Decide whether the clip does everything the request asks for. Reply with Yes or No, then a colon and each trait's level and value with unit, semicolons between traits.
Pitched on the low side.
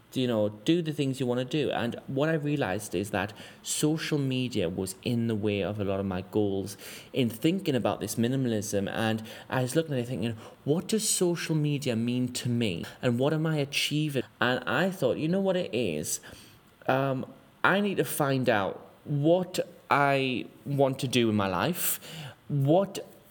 Yes: low, 130 Hz